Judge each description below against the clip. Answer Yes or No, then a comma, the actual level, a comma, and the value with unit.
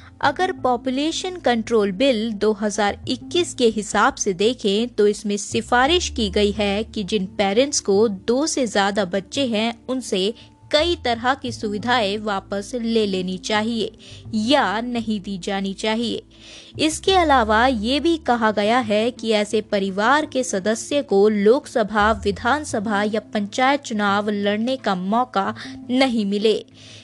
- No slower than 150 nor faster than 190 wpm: No, average, 135 wpm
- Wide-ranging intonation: No, average, 3.8 semitones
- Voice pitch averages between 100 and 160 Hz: No, high, 220 Hz